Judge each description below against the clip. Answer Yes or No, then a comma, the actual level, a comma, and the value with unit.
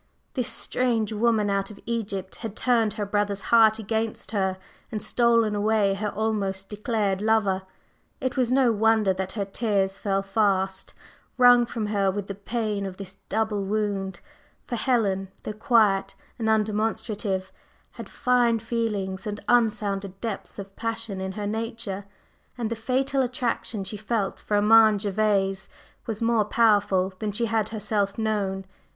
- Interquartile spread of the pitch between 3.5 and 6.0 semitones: No, narrow, 2.5 semitones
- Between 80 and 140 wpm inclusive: No, average, 150 wpm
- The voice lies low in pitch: No, high, 210 Hz